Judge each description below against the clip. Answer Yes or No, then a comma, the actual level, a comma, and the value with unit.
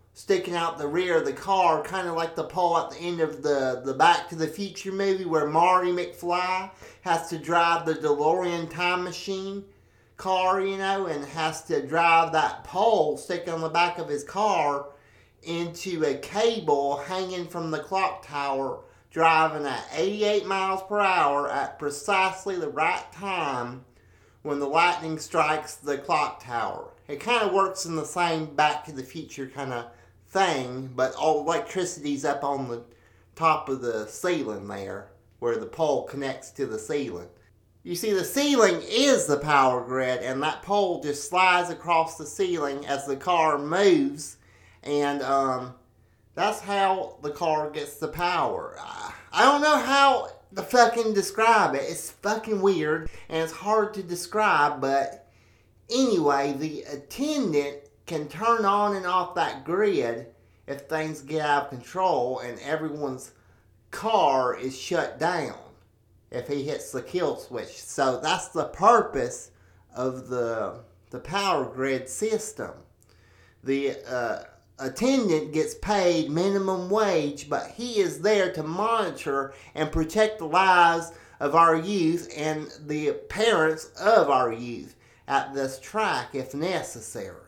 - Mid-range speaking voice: Yes, medium, 160 Hz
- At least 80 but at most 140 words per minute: No, average, 155 wpm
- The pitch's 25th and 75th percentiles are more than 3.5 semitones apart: Yes, average, 5.3 semitones